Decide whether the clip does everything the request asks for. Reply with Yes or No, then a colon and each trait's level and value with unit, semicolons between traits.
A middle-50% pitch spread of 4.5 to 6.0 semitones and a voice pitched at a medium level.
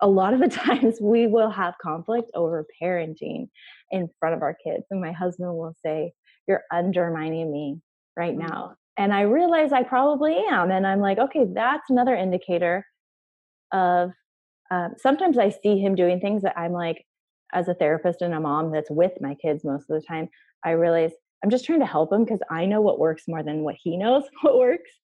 Yes: wide, 5.4 semitones; medium, 180 Hz